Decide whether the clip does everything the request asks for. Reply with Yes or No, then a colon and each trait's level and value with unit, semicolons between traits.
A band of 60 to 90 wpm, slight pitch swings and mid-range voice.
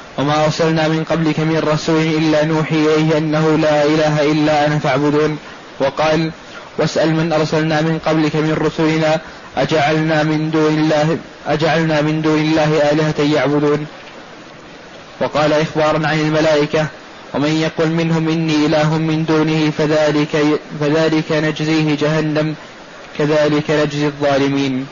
No: average, 125 wpm; narrow, 0.7 semitones; medium, 155 Hz